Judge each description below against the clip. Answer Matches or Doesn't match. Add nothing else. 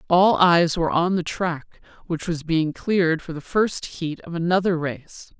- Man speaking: Doesn't match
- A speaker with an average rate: Matches